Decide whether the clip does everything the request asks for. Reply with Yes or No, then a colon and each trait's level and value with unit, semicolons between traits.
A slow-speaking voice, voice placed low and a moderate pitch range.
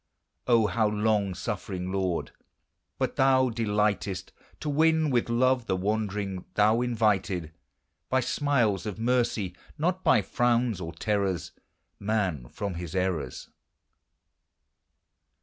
Yes: slow, 115 wpm; low, 105 Hz; average, 4.3 semitones